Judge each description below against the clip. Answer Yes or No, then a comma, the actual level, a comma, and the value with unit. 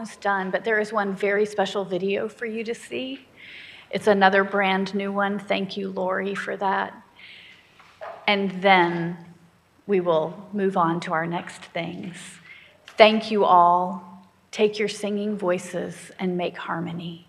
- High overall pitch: Yes, high, 195 Hz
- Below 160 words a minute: Yes, average, 145 wpm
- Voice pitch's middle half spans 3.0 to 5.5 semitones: No, narrow, 2.5 semitones